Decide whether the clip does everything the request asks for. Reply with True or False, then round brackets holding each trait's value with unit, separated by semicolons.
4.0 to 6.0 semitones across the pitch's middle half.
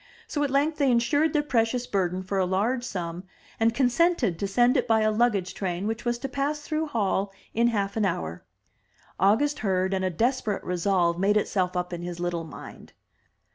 True (5.2 semitones)